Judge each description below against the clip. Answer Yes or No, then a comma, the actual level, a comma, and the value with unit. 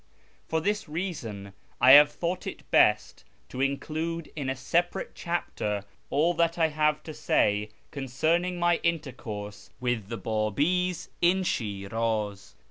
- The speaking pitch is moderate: Yes, medium, 145 Hz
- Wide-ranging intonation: Yes, wide, 7.3 semitones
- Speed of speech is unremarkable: No, slow, 130 wpm